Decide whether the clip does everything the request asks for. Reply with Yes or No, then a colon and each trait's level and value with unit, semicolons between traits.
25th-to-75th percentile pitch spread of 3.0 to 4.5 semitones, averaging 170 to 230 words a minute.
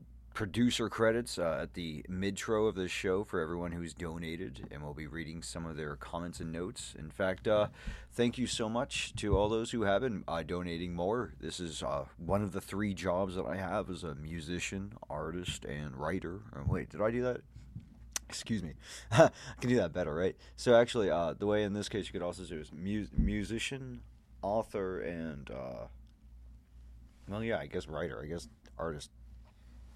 No: average, 5.0 semitones; average, 190 wpm